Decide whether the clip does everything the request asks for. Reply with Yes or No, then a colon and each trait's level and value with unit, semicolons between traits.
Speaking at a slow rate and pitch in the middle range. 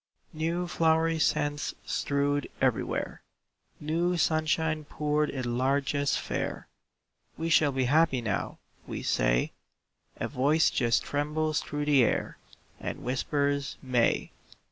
Yes: slow, 115 wpm; medium, 145 Hz